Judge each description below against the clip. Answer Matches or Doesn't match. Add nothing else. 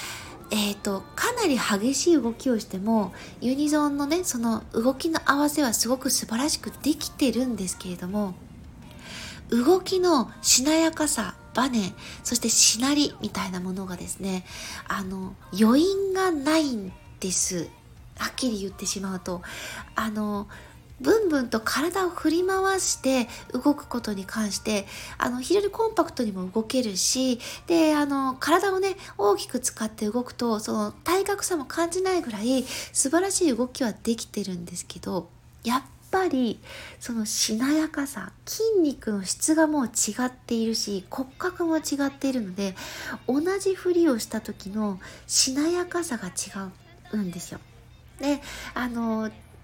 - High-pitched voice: Matches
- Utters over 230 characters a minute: Matches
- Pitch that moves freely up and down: Matches